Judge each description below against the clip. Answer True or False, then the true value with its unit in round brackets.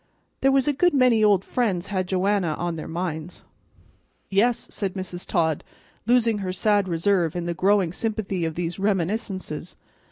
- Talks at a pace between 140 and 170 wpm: True (160 wpm)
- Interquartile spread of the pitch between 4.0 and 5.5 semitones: False (3.6 semitones)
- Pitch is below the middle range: False (190 Hz)